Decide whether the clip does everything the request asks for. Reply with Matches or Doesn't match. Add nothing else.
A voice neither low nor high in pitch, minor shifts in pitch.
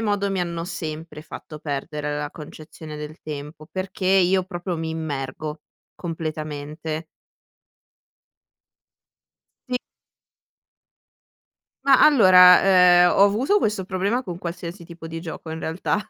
Doesn't match